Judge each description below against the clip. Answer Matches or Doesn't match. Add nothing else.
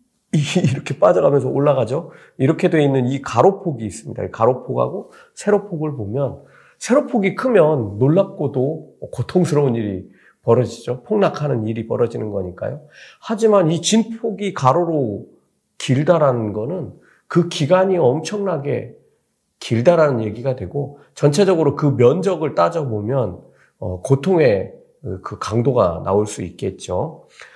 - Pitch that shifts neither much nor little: Doesn't match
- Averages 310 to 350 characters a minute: Doesn't match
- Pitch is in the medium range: Matches